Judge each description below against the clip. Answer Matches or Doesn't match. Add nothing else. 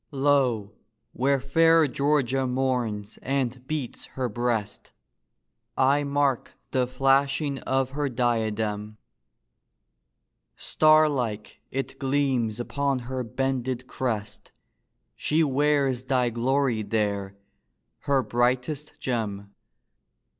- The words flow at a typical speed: Doesn't match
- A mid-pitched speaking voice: Doesn't match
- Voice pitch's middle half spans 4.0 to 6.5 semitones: Doesn't match